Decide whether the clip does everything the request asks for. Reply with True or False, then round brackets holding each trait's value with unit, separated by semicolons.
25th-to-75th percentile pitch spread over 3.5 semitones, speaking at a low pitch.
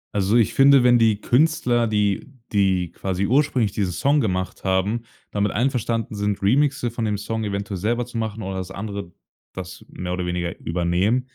True (4.0 semitones; 105 Hz)